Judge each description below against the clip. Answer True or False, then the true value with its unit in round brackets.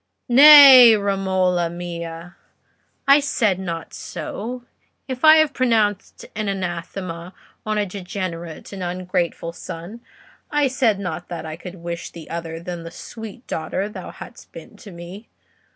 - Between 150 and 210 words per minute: False (140 wpm)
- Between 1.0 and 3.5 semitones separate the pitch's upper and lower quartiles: False (4.6 semitones)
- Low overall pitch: False (190 Hz)